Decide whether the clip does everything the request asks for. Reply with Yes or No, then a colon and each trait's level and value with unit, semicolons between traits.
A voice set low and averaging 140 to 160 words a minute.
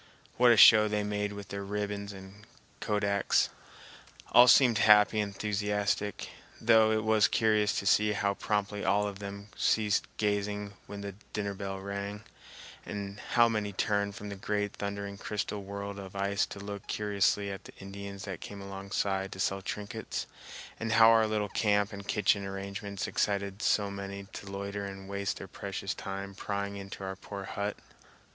No: low, 100 Hz; average, 170 wpm